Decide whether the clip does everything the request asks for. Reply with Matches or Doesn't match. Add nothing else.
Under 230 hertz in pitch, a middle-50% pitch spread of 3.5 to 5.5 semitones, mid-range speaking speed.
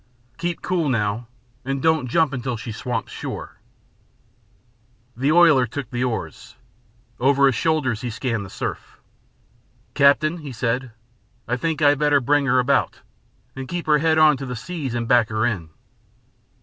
Matches